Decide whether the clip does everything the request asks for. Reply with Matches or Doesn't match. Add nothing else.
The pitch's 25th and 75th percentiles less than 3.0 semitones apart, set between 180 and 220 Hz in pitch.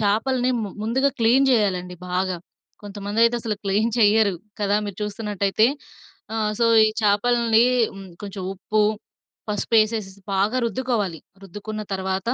Matches